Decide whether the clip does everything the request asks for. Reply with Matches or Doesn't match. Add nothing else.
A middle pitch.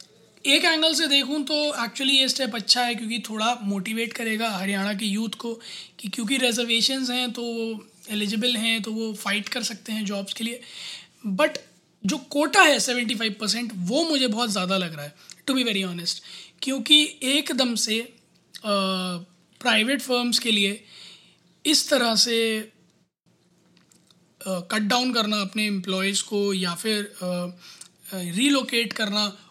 Doesn't match